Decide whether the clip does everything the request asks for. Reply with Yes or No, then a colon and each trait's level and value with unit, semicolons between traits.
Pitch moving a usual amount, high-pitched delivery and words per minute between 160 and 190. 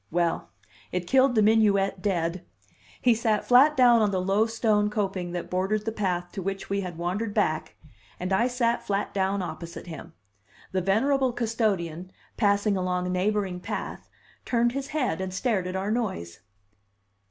Yes: average, 3.8 semitones; high, 200 Hz; average, 165 wpm